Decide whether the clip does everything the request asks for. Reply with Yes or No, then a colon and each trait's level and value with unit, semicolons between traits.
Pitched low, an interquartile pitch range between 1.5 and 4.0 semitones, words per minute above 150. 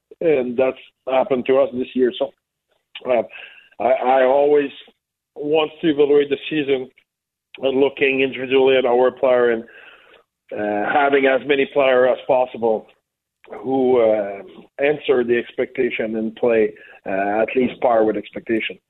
No: low, 130 Hz; average, 3.2 semitones; average, 140 wpm